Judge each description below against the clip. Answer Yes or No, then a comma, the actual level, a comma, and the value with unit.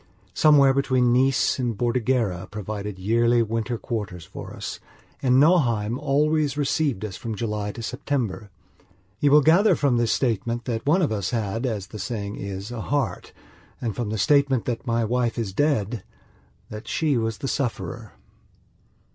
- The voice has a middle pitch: No, low, 120 Hz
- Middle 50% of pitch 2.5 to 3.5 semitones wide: No, average, 4.1 semitones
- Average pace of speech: Yes, average, 160 wpm